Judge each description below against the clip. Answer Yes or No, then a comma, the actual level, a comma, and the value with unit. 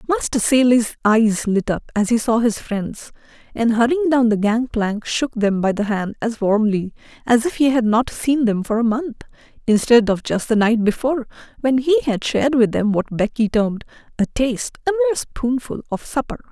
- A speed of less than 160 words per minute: No, average, 195 wpm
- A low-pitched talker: No, high, 235 Hz